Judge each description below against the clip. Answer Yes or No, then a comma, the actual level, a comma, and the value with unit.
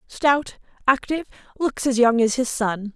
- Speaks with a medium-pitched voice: No, very high, 250 Hz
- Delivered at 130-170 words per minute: Yes, average, 140 wpm